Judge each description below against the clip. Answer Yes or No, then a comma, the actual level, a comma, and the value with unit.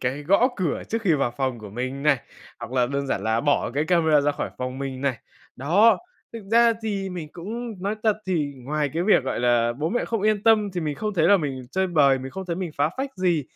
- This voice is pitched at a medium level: Yes, medium, 155 Hz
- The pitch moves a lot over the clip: Yes, wide, 6.6 semitones